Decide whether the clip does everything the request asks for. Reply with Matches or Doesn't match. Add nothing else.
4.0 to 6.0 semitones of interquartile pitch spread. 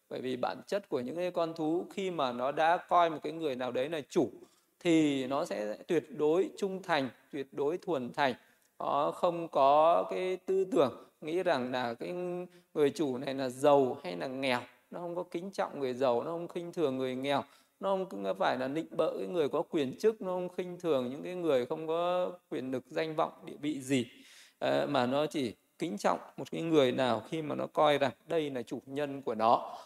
Matches